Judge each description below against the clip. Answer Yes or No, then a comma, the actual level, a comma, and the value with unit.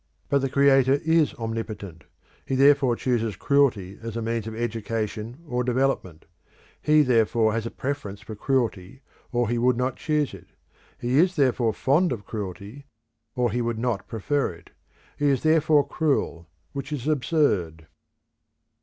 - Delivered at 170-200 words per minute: No, average, 155 wpm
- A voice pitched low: Yes, low, 120 Hz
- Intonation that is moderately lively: Yes, average, 4.2 semitones